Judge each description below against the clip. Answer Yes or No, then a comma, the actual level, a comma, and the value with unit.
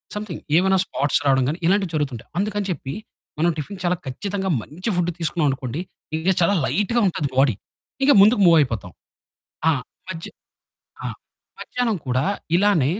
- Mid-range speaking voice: Yes, medium, 175 Hz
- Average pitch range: No, wide, 6.0 semitones